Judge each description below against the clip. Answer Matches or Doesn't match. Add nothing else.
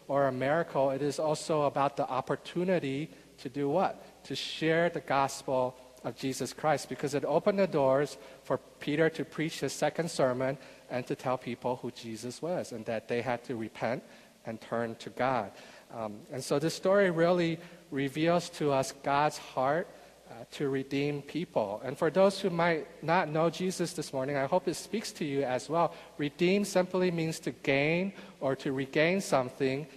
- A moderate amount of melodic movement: Matches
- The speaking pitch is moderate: Matches